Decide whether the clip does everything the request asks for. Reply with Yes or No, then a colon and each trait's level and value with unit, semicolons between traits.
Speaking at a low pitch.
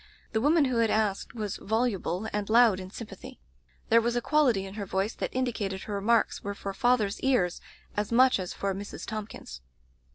No: high, 215 Hz